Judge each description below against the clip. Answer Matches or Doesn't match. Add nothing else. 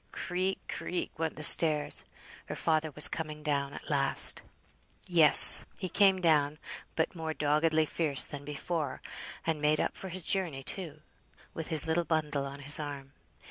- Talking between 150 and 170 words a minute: Matches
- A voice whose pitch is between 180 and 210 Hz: Doesn't match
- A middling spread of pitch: Doesn't match